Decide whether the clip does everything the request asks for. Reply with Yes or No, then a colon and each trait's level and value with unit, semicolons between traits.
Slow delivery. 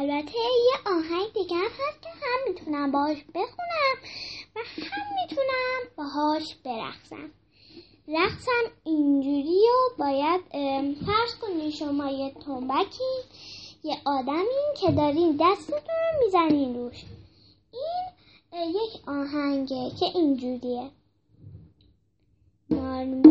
Yes: slow, 95 wpm